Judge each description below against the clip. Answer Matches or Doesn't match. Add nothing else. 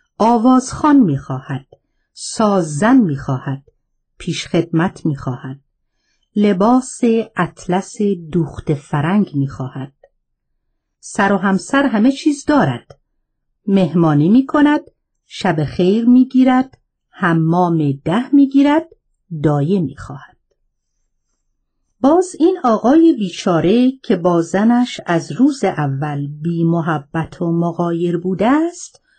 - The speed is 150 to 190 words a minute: Doesn't match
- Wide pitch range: Matches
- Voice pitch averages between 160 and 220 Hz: Matches